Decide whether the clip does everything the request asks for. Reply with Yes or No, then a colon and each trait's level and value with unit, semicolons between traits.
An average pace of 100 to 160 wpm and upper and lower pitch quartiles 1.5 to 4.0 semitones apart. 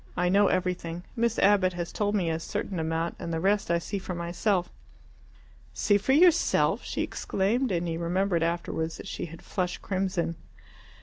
No: average, 175 wpm; average, 3.0 semitones